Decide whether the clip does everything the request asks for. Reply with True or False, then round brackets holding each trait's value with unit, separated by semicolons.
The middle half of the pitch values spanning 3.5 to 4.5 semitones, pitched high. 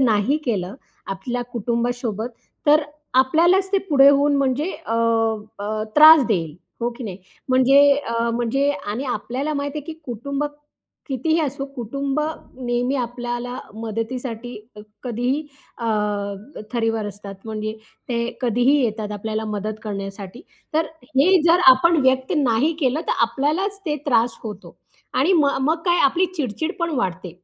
True (4.2 semitones; 250 Hz)